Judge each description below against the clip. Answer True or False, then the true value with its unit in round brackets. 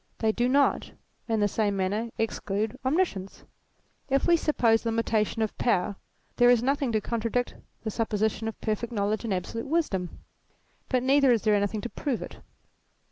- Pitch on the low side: False (225 Hz)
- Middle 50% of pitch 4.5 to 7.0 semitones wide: False (2.8 semitones)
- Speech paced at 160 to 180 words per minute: True (165 wpm)